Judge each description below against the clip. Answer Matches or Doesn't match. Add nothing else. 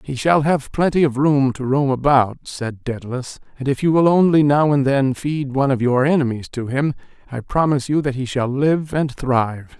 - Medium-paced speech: Doesn't match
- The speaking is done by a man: Matches